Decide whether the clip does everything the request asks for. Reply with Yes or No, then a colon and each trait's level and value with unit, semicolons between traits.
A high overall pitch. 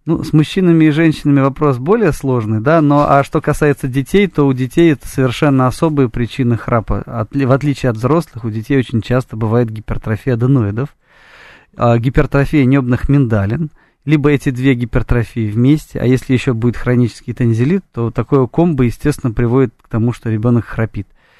No: low, 130 Hz